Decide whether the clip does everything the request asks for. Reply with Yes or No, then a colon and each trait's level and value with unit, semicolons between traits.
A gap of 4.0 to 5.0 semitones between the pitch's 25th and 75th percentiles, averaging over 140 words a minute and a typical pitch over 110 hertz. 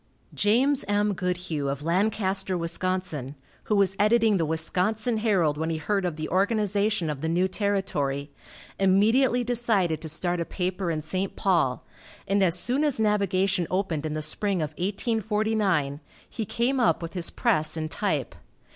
Yes: average, 4.4 semitones; average, 160 wpm; high, 190 Hz